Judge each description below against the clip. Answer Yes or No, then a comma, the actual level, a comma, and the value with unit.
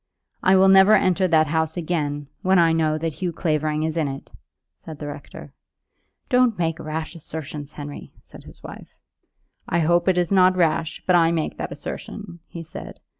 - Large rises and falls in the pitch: No, average, 2.8 semitones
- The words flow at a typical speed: Yes, average, 180 wpm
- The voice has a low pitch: No, medium, 165 Hz